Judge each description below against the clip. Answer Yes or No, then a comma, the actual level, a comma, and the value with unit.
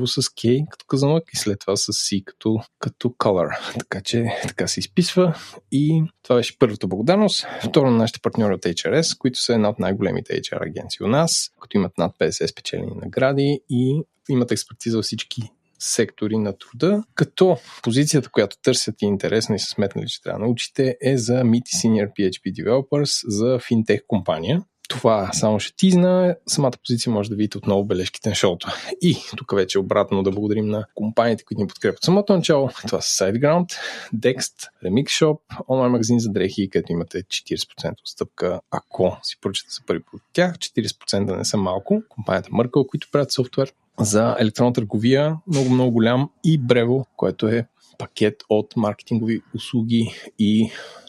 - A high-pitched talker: No, low, 120 Hz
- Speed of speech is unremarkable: No, fast, 175 wpm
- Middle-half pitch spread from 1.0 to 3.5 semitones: No, average, 4.9 semitones